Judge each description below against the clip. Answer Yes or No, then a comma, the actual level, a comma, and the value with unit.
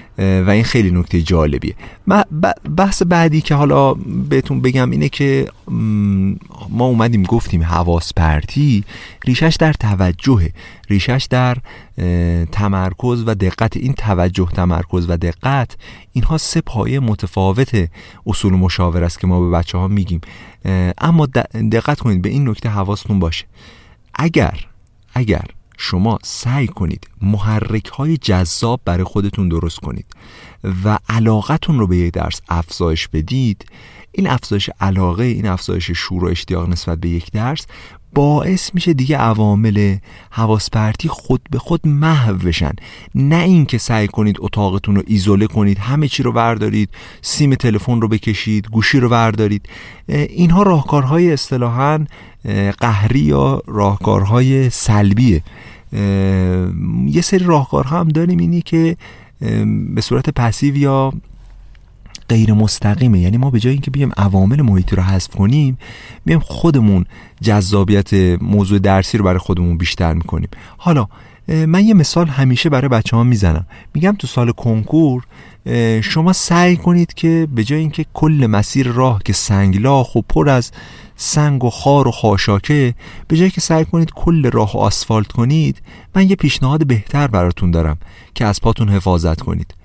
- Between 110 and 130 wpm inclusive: No, average, 140 wpm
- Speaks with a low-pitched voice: Yes, low, 110 Hz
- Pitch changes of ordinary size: No, wide, 6.1 semitones